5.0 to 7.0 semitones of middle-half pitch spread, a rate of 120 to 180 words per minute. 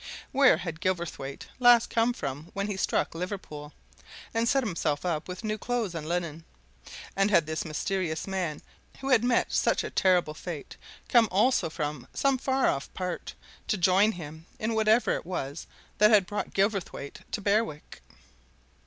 Yes: wide, 5.5 semitones; average, 160 wpm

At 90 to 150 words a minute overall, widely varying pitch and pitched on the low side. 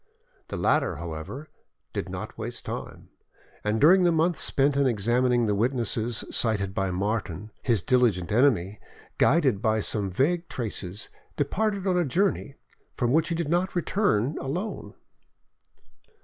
Yes: average, 140 wpm; wide, 7.5 semitones; low, 125 Hz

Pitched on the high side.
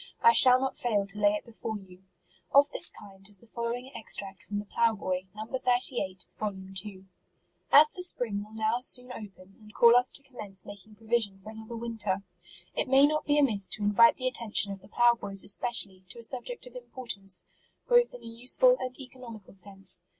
Yes: high, 220 Hz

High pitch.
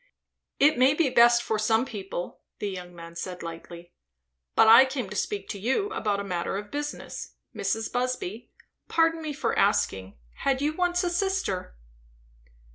Yes: high, 225 Hz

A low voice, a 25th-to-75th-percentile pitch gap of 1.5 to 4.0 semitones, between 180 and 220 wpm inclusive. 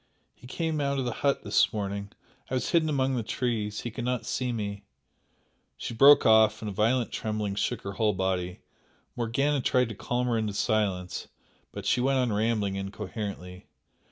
Yes: low, 110 Hz; average, 3.7 semitones; average, 190 wpm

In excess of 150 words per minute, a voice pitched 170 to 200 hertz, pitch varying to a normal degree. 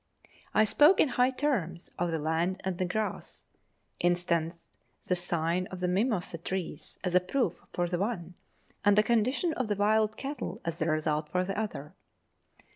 Yes: average, 175 wpm; medium, 185 Hz; average, 4.2 semitones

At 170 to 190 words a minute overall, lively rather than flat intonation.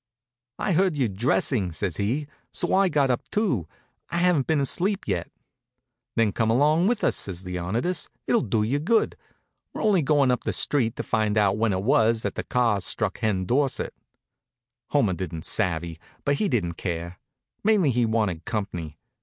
Yes: average, 175 wpm; wide, 7.5 semitones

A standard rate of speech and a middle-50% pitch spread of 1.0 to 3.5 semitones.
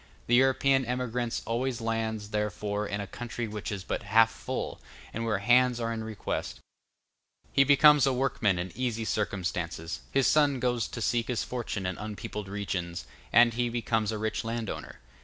Yes: average, 170 wpm; average, 2.9 semitones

